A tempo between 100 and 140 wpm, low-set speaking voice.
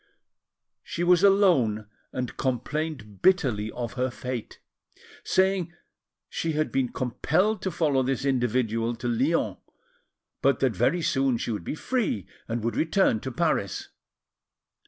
Yes: slow, 135 wpm; low, 130 Hz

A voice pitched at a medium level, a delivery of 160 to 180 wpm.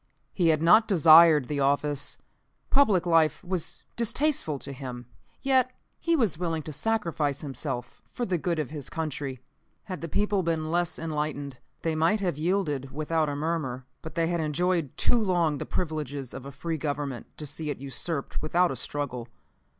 Yes: medium, 155 Hz; average, 175 wpm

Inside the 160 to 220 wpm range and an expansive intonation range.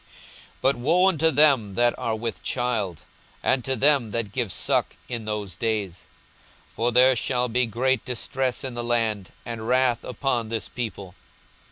No: average, 165 wpm; average, 2.9 semitones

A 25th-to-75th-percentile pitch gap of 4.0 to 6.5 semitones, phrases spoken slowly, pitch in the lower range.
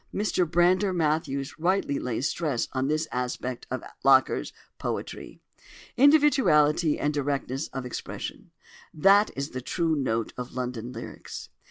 No: average, 5.1 semitones; slow, 125 wpm; medium, 145 Hz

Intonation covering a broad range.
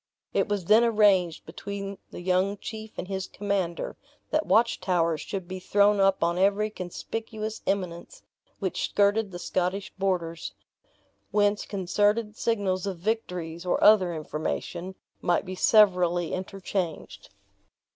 No: average, 2.7 semitones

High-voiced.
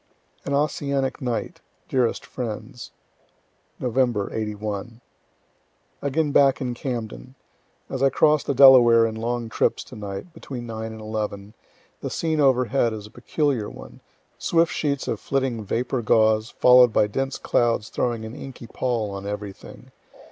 No: low, 120 Hz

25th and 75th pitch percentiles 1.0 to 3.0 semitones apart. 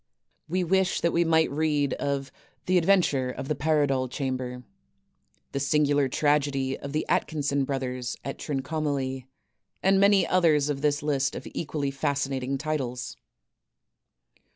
Yes: narrow, 2.6 semitones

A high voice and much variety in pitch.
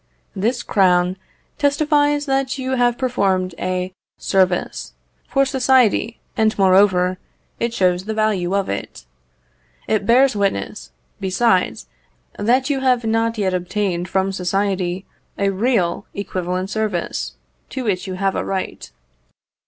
No: high, 200 Hz; average, 4.7 semitones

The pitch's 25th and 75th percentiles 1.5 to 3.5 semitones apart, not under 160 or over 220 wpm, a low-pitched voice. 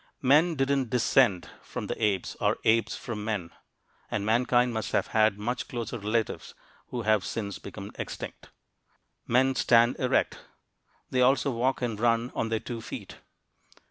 No: narrow, 2.6 semitones; average, 150 wpm; low, 115 Hz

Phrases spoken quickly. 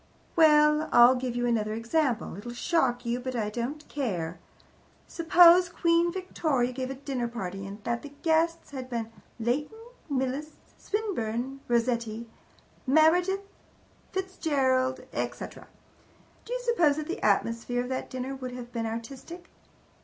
No: average, 140 wpm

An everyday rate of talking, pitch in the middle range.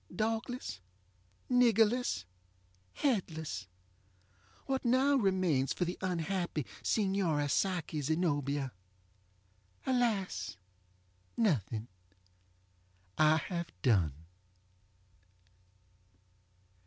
No: slow, 55 wpm; medium, 170 Hz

